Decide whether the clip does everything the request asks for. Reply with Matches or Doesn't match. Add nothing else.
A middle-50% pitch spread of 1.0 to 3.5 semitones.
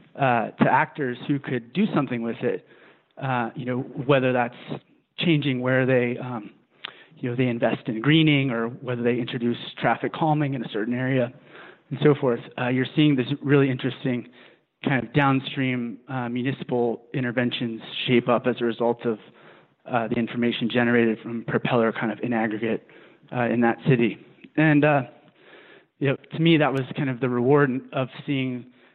Matches